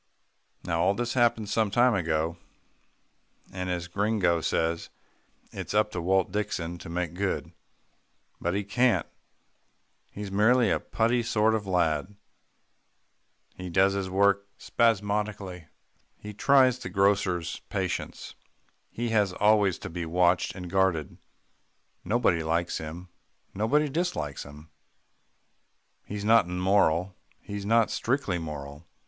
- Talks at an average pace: No, slow, 125 wpm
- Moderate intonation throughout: Yes, average, 3.6 semitones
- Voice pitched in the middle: No, very low, 95 Hz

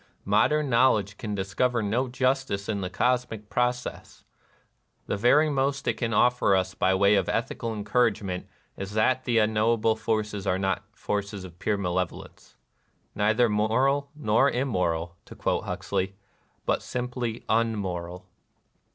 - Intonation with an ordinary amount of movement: Yes, average, 3.9 semitones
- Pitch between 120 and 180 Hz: No, low, 110 Hz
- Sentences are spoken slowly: No, average, 155 wpm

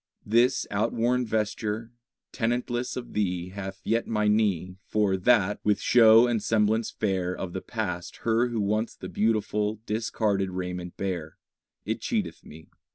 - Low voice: Yes, low, 105 Hz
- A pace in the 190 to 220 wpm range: No, average, 145 wpm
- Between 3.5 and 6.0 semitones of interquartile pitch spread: No, average, 3.0 semitones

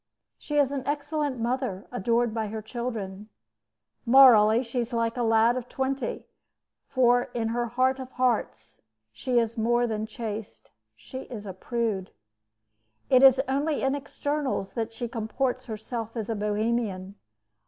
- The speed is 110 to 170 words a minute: Yes, average, 150 wpm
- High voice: Yes, high, 235 Hz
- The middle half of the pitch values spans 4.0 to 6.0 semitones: No, average, 3.0 semitones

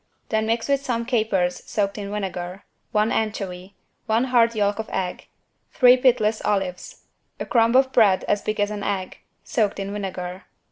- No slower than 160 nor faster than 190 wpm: Yes, average, 170 wpm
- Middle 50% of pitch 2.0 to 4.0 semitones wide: Yes, average, 2.9 semitones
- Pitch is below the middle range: No, high, 210 Hz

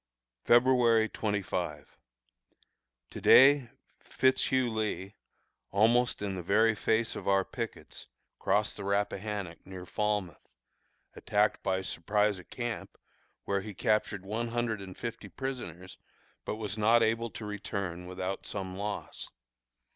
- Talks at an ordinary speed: No, slow, 125 wpm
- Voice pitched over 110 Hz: No, low, 105 Hz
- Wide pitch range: No, average, 3.1 semitones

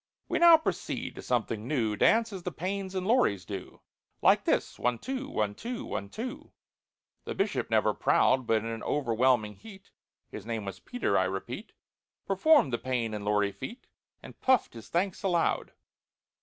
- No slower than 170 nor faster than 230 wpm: No, average, 160 wpm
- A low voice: Yes, low, 130 Hz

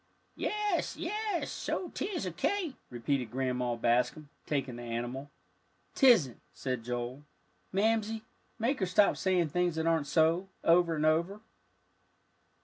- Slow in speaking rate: Yes, slow, 130 wpm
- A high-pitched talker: No, medium, 160 Hz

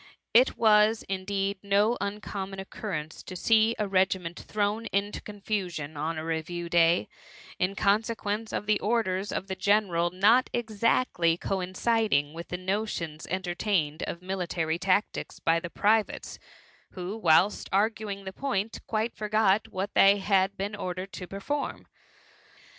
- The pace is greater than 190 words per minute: No, average, 140 wpm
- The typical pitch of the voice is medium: No, high, 195 Hz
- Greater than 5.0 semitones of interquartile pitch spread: No, average, 2.9 semitones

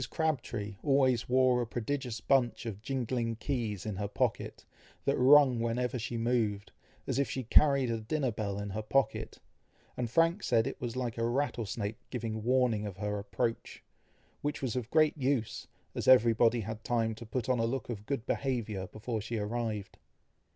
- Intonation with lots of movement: No, average, 3.0 semitones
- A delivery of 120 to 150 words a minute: No, average, 175 wpm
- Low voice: Yes, low, 120 Hz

